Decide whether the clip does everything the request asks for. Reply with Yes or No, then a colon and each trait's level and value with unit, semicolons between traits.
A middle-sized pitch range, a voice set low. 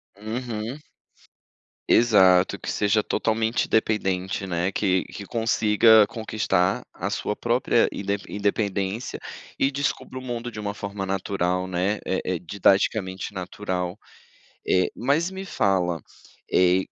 Yes: average, 3.0 semitones; low, 100 Hz